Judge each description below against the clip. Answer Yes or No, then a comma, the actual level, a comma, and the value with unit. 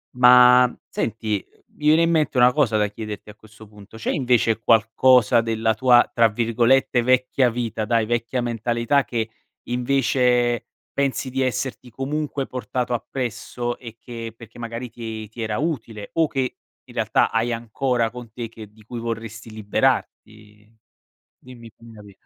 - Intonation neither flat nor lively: No, narrow, 2.2 semitones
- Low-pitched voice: Yes, low, 120 Hz